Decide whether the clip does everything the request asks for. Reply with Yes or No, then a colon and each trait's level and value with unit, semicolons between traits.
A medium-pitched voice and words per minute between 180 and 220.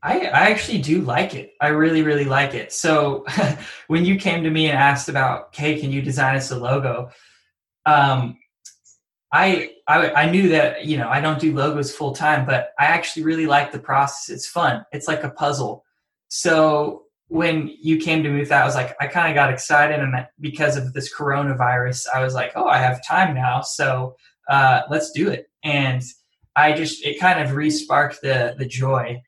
Yes: medium, 145 Hz; fast, 205 wpm